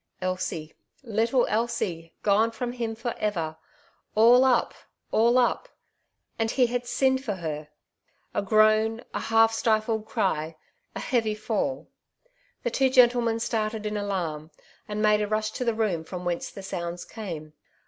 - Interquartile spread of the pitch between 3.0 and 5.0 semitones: Yes, average, 3.7 semitones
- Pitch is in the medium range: No, high, 215 Hz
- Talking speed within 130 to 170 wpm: Yes, average, 160 wpm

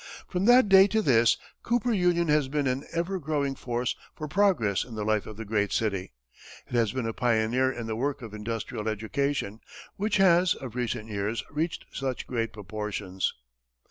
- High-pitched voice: No, low, 125 Hz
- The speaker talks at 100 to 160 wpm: No, average, 180 wpm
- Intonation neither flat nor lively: No, wide, 7.1 semitones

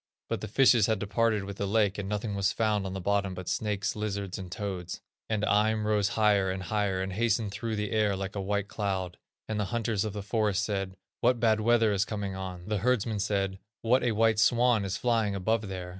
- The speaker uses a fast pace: Yes, fast, 225 wpm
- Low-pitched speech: Yes, low, 105 Hz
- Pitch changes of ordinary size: No, narrow, 2.2 semitones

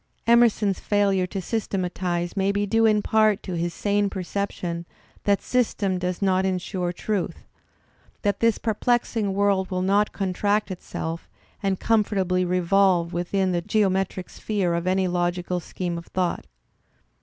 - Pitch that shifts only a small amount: Yes, narrow, 2.3 semitones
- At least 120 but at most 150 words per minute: Yes, average, 140 wpm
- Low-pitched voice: No, high, 190 Hz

